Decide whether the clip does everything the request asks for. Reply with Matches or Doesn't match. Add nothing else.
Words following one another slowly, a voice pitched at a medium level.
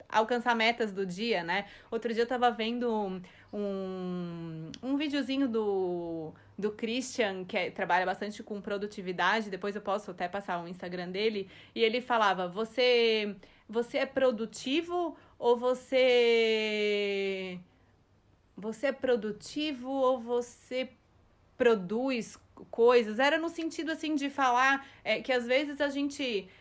Doesn't match